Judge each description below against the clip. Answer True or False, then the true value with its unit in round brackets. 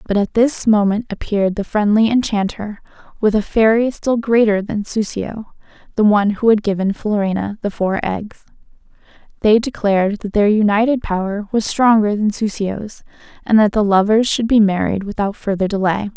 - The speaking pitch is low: False (210 Hz)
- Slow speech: False (165 wpm)